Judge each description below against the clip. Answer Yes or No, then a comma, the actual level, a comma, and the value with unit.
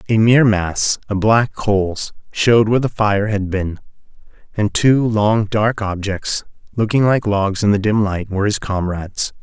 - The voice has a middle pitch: No, low, 105 Hz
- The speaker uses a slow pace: No, average, 170 wpm